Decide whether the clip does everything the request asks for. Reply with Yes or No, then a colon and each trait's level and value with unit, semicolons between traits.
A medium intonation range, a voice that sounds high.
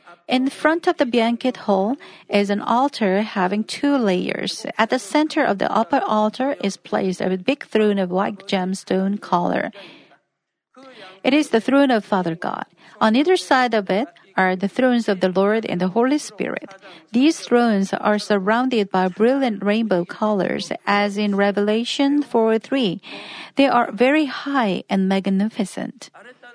Yes: average, 4.6 semitones; high, 215 Hz